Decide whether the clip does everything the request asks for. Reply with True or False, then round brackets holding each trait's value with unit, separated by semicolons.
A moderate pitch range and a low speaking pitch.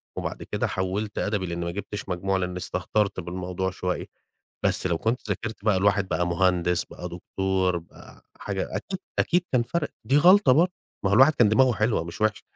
True (3.6 semitones; 95 Hz)